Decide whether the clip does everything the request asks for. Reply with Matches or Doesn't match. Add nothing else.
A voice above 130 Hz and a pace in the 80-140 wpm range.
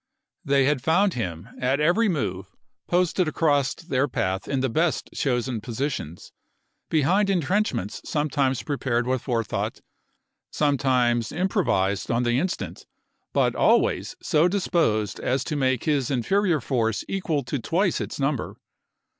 Matches